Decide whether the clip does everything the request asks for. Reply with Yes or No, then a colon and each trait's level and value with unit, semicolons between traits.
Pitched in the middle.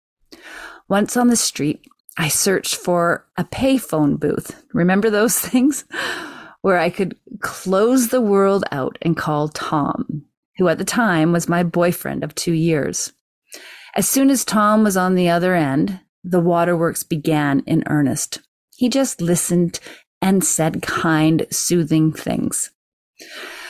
Yes: medium, 175 Hz